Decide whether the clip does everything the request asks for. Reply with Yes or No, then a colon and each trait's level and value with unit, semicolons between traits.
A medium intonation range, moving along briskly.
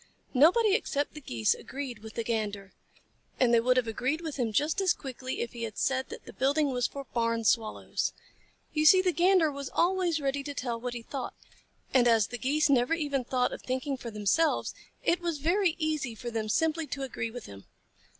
Yes: average, 4.9 semitones; fast, 210 wpm